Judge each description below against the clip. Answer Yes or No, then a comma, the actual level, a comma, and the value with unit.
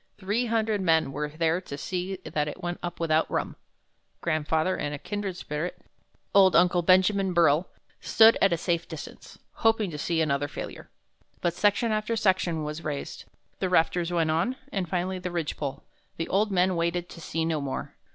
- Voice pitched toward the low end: No, medium, 175 Hz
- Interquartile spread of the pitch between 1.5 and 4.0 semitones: Yes, average, 3.0 semitones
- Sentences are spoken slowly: No, average, 180 wpm